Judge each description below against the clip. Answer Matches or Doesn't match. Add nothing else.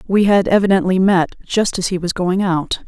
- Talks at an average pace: Doesn't match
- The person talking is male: Doesn't match